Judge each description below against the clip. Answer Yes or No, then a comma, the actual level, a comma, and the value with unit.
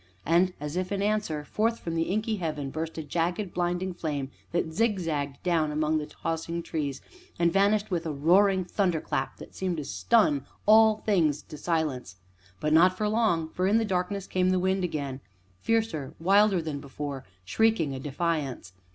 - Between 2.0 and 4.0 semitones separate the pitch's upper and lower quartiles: No, average, 4.4 semitones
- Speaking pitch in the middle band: Yes, medium, 170 Hz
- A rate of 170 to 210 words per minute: Yes, average, 175 wpm